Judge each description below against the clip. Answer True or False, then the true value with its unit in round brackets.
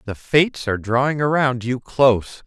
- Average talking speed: True (170 wpm)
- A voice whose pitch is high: False (125 Hz)